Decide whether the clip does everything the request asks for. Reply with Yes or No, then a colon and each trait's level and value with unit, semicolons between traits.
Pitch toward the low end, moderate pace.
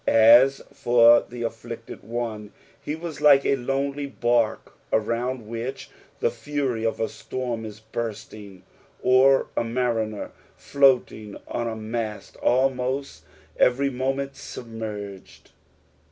No: low, 120 Hz; slow, 115 wpm